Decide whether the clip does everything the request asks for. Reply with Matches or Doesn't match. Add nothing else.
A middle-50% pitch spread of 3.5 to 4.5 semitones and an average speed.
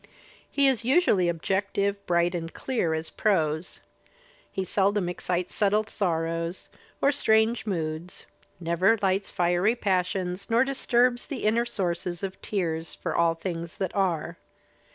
Doesn't match